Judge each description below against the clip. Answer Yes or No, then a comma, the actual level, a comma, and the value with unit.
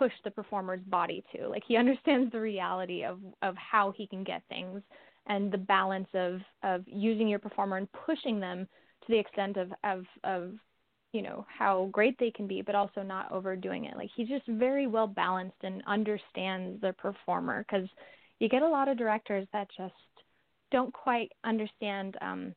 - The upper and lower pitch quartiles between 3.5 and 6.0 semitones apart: No, average, 2.9 semitones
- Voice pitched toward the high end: Yes, high, 200 Hz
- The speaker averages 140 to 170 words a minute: No, average, 185 wpm